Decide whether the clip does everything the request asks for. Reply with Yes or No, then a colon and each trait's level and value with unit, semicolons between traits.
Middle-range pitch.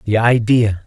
No: low, 110 Hz